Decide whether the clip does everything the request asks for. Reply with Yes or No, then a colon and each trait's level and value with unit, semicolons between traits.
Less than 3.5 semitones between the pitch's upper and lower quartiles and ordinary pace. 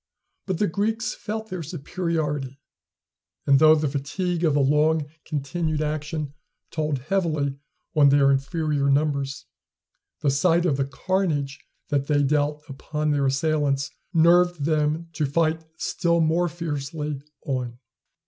No: average, 3.0 semitones; slow, 130 wpm